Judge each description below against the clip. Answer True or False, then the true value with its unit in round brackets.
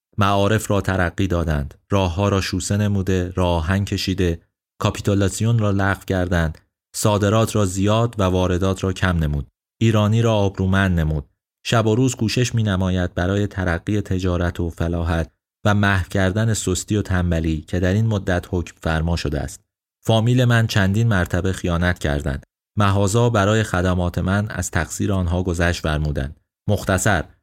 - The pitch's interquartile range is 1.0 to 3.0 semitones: True (2.7 semitones)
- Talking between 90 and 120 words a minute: False (150 wpm)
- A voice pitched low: True (95 Hz)